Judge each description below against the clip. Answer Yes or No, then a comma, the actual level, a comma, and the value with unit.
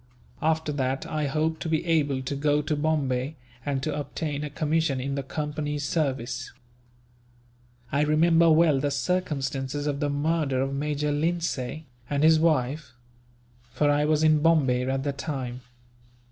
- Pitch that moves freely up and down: No, narrow, 2.4 semitones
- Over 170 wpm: No, average, 155 wpm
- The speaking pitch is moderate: Yes, medium, 145 Hz